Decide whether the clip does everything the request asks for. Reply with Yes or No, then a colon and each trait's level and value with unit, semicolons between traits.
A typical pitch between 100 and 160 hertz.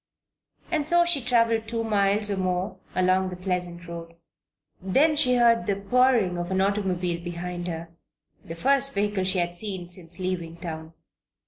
No: high, 190 Hz